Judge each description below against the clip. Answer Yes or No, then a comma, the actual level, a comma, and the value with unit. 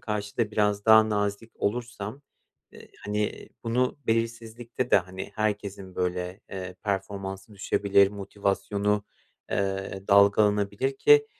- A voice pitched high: No, low, 105 Hz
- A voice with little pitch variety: Yes, narrow, 2.2 semitones